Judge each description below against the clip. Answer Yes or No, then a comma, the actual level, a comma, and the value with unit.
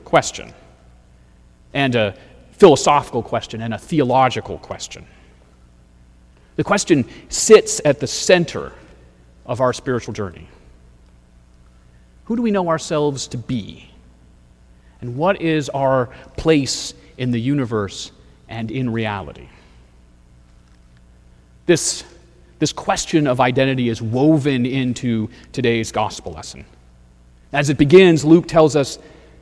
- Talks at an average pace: No, slow, 110 wpm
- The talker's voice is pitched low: Yes, low, 110 Hz